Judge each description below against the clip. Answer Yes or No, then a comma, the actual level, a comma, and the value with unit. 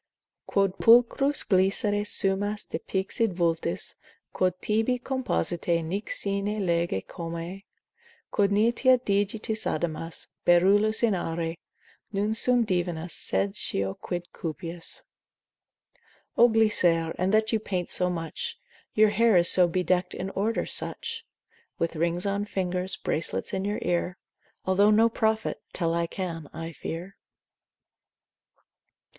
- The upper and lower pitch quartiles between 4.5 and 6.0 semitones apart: No, average, 3.8 semitones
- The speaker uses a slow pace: Yes, slow, 125 wpm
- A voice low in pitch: No, high, 190 Hz